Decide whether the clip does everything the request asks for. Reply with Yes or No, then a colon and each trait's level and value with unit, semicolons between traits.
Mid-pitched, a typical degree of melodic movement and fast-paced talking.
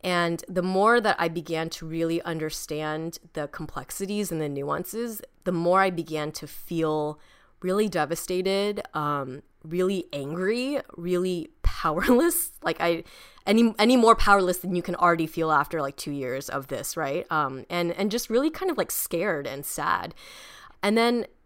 No: medium, 175 Hz; average, 4.3 semitones; average, 160 wpm